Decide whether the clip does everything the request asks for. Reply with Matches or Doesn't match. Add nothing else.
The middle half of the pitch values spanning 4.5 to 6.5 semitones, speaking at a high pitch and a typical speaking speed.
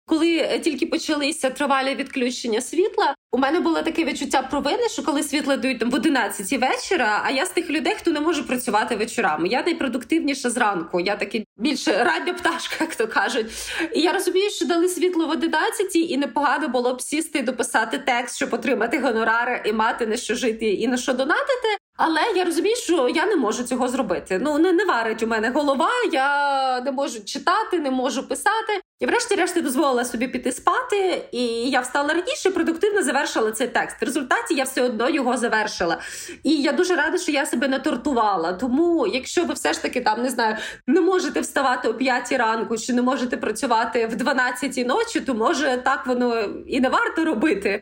Doesn't match